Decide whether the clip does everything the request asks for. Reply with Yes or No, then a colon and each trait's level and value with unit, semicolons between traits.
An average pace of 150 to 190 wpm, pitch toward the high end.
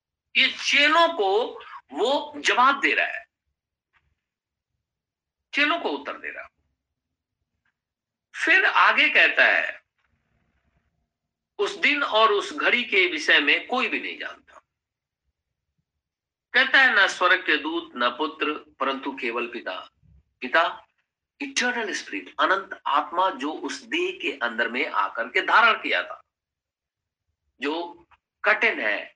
No: average, 125 wpm; very high, 285 Hz